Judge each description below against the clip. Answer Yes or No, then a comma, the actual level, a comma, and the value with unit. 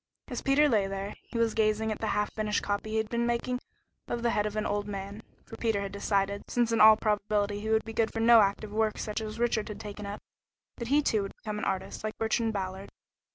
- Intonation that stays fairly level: Yes, narrow, 1.7 semitones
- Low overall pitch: No, high, 215 Hz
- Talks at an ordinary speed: No, fast, 245 wpm